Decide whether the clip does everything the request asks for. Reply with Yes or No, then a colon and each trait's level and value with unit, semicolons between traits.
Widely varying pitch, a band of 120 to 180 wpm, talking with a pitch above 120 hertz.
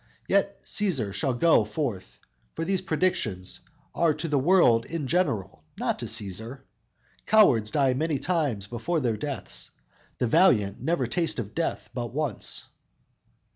Yes: wide, 7.1 semitones; average, 140 wpm; low, 135 Hz